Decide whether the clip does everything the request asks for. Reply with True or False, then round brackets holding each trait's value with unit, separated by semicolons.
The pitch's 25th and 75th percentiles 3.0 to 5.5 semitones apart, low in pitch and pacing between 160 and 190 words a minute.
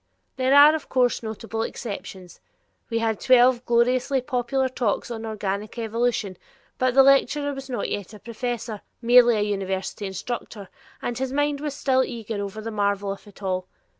False (3.8 semitones; 235 Hz; 165 wpm)